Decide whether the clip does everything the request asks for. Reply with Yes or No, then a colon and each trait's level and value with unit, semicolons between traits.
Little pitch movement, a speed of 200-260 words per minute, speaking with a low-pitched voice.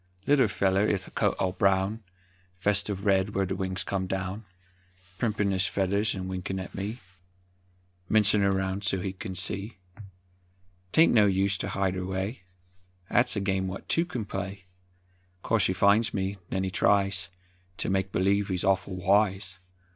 No: narrow, 1.4 semitones; average, 160 wpm; very low, 95 Hz